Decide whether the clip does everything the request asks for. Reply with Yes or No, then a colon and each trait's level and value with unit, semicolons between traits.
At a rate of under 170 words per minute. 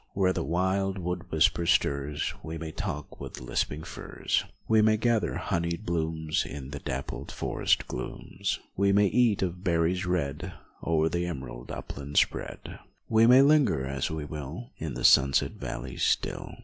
Yes: average, 160 wpm